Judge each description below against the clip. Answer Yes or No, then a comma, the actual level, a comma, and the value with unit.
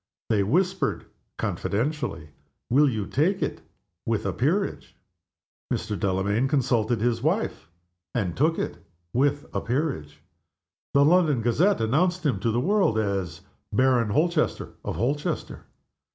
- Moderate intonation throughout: No, wide, 6.1 semitones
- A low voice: Yes, low, 130 Hz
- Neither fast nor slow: No, slow, 125 wpm